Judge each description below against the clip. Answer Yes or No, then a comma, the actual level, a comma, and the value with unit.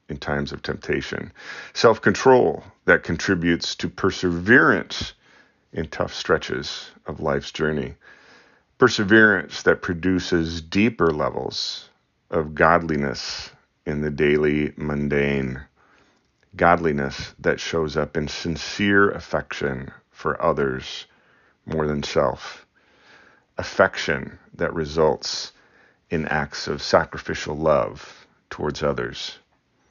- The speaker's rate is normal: No, slow, 100 wpm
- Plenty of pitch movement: No, average, 3.6 semitones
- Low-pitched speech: Yes, very low, 75 Hz